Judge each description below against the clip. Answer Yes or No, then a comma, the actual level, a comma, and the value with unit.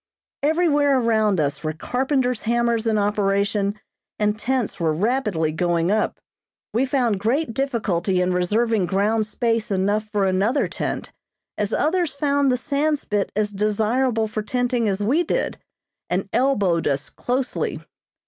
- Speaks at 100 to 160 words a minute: Yes, average, 140 wpm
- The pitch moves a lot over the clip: No, average, 4.4 semitones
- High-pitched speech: Yes, high, 220 Hz